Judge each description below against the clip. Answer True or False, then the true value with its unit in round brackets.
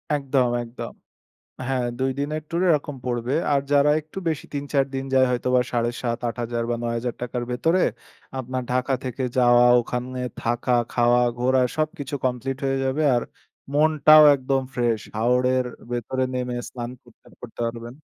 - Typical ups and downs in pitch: False (2.2 semitones)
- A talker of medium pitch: False (125 Hz)